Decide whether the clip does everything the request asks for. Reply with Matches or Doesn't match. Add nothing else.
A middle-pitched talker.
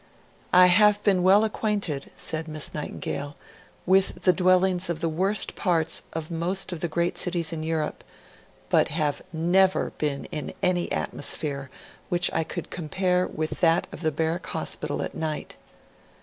Matches